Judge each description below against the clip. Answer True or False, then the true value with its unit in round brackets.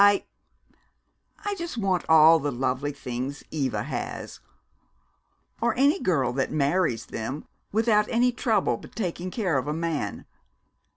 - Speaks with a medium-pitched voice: True (165 Hz)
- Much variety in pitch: True (7.6 semitones)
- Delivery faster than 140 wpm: False (135 wpm)